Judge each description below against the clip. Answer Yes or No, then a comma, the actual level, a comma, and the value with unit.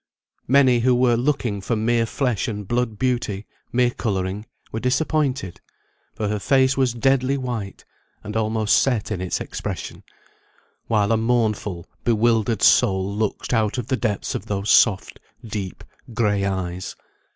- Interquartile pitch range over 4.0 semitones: No, average, 3.4 semitones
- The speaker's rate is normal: Yes, average, 145 wpm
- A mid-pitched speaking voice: No, low, 110 Hz